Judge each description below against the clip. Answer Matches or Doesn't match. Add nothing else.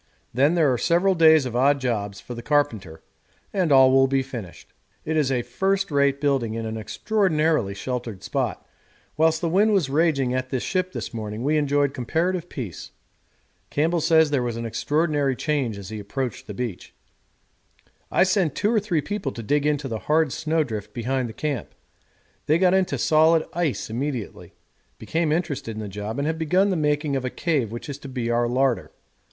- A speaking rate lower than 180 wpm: Doesn't match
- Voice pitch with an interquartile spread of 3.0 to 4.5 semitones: Doesn't match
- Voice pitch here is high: Doesn't match